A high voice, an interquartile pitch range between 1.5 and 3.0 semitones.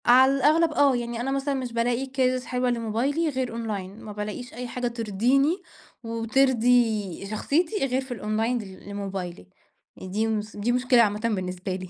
No: high, 235 Hz; average, 3.6 semitones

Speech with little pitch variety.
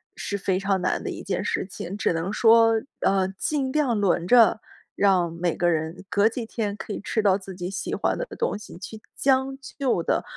No: average, 3.7 semitones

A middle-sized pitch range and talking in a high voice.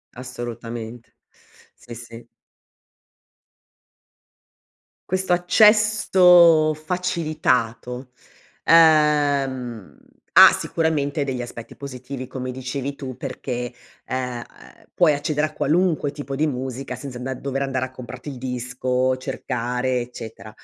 No: average, 3.6 semitones; low, 130 Hz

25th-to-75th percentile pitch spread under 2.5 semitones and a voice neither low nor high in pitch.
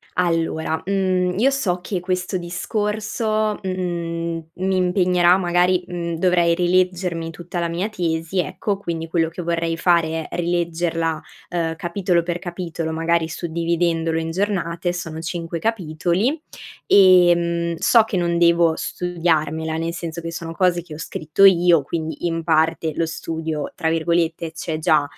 Yes: narrow, 1.7 semitones; medium, 170 Hz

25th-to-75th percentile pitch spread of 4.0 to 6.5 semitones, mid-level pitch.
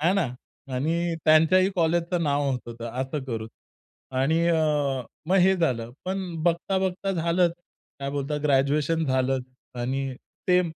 Yes: average, 4.3 semitones; medium, 160 Hz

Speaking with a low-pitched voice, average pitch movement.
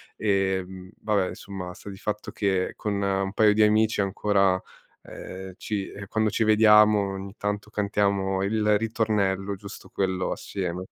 No: low, 100 Hz; narrow, 1.8 semitones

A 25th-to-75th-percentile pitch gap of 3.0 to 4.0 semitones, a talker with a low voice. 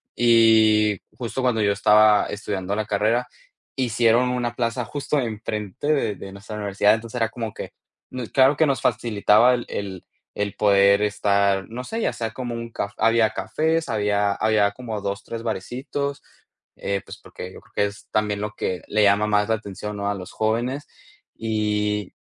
No: narrow, 2.5 semitones; low, 110 Hz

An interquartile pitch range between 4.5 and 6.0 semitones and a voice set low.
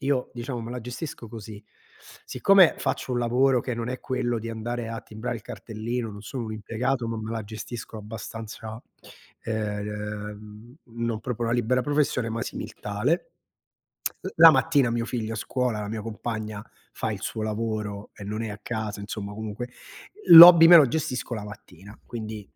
No: narrow, 2.6 semitones; low, 115 Hz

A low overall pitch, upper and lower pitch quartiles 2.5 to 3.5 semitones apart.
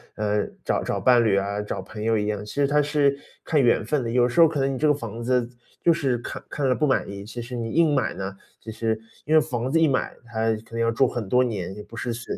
No: low, 120 Hz; average, 3.9 semitones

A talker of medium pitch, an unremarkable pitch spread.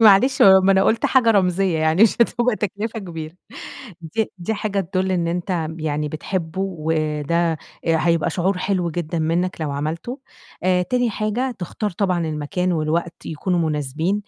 Yes: medium, 180 Hz; average, 3.6 semitones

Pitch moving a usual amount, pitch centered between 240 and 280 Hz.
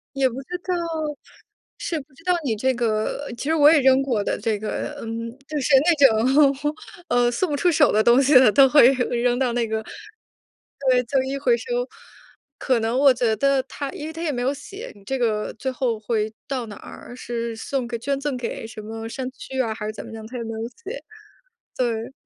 Yes: average, 3.6 semitones; very high, 255 Hz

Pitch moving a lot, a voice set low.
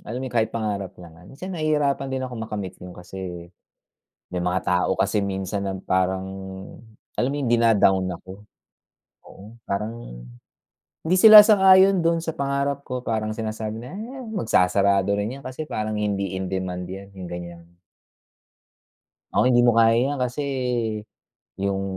Yes: wide, 6.1 semitones; low, 110 Hz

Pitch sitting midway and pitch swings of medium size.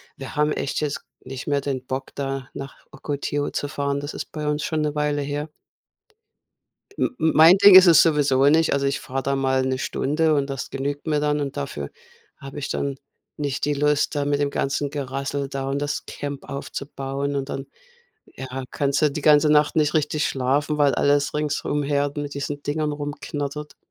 No: medium, 145 Hz; narrow, 1.3 semitones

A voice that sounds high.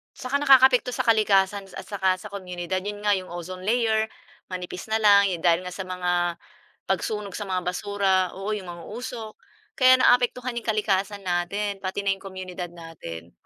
Yes: high, 195 Hz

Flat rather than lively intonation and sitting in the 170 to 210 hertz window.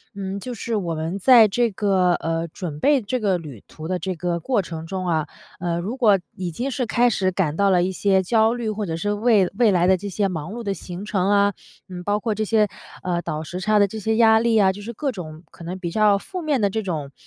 No: average, 3.8 semitones; high, 195 Hz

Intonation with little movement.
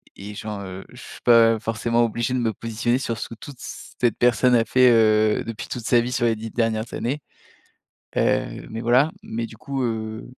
Yes: narrow, 1.7 semitones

